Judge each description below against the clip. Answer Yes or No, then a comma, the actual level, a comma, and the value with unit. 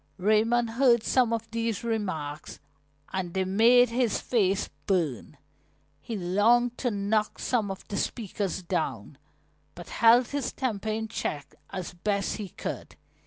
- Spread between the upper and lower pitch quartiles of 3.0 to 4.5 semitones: Yes, average, 3.6 semitones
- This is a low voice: No, high, 215 Hz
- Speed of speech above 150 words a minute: No, average, 140 wpm